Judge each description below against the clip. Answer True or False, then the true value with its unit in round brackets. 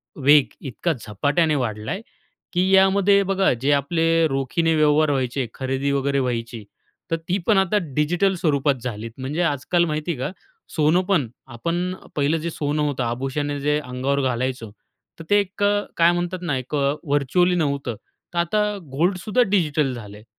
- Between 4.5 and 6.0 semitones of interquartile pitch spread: True (4.8 semitones)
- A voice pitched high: False (150 Hz)